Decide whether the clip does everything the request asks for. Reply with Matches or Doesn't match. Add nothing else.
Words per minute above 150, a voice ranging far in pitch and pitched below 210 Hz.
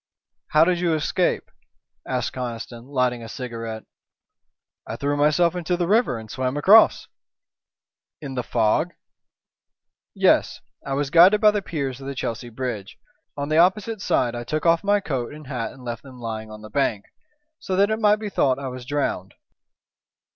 Matches